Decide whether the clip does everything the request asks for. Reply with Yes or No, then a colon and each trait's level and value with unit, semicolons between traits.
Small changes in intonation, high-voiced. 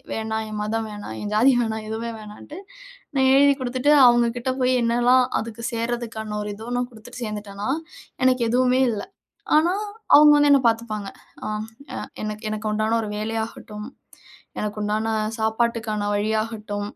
Yes: narrow, 2.3 semitones; high, 225 Hz